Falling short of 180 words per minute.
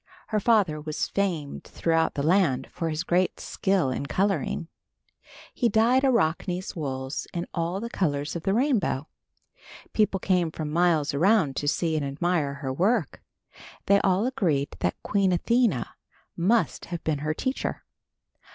Yes: average, 150 wpm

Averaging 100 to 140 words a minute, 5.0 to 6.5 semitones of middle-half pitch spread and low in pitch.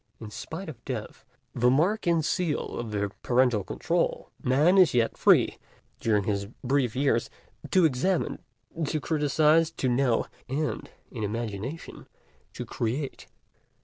Yes: slow, 135 wpm; wide, 5.5 semitones; low, 130 Hz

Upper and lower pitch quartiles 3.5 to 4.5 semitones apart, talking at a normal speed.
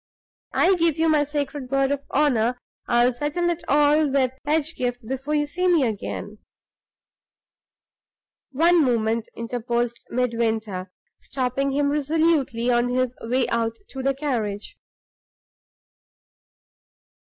No: average, 3.8 semitones; slow, 115 wpm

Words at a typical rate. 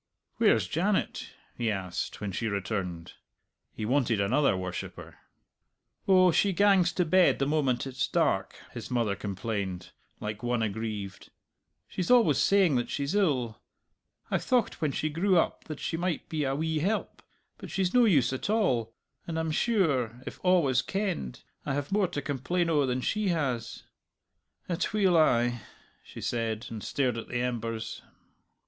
Yes: average, 160 wpm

